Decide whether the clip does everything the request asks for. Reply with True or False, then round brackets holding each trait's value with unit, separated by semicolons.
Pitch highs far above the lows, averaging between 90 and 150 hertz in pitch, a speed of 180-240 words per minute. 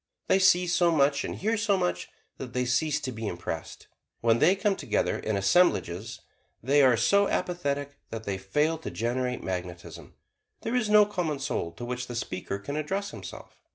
True (8.1 semitones; 140 Hz; 185 wpm)